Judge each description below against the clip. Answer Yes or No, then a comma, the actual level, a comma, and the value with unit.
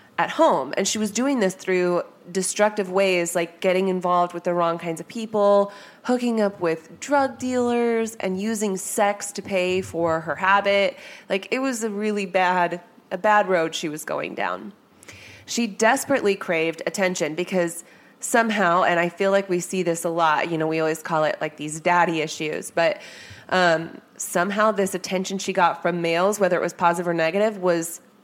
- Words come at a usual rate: Yes, average, 185 wpm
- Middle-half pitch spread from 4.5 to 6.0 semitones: No, average, 3.4 semitones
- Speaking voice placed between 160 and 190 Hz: Yes, medium, 185 Hz